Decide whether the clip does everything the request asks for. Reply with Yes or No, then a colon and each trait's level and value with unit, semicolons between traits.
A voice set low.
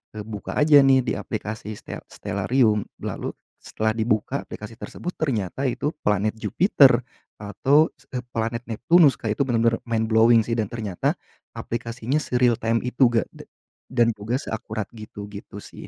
Yes: low, 115 Hz